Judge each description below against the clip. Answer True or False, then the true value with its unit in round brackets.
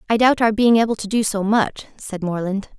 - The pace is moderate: False (235 wpm)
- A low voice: False (215 Hz)